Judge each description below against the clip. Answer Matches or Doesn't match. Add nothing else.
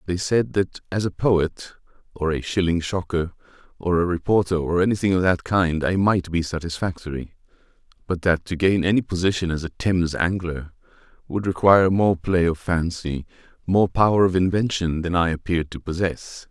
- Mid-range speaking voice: Doesn't match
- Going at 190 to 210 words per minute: Doesn't match